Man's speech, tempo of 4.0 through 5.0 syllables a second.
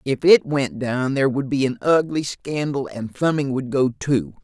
Yes: male; 4.6 syllables/s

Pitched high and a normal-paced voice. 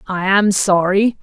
Yes: high, 195 Hz; average, 145 wpm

